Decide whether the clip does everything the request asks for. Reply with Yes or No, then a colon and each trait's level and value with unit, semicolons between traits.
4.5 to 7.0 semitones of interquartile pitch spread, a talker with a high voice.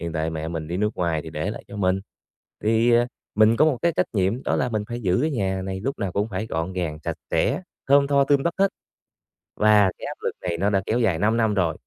No: average, 4.8 semitones; low, 100 Hz